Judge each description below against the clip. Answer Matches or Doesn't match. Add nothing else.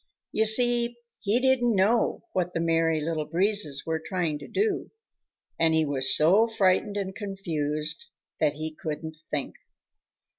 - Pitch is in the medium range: Matches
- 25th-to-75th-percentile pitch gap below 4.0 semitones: Doesn't match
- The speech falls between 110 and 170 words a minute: Matches